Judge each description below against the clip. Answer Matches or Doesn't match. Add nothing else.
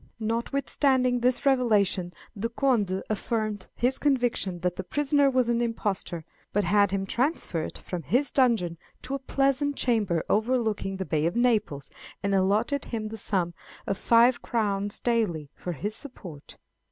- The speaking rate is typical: Matches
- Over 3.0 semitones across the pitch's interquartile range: Matches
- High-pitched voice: Matches